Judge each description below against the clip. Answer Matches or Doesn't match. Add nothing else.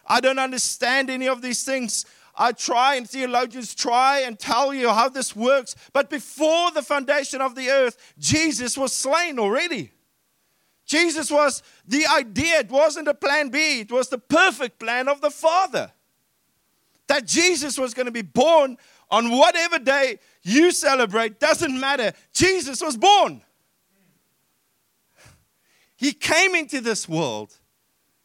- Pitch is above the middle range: Matches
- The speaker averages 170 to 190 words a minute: Doesn't match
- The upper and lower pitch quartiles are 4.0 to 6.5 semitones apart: Doesn't match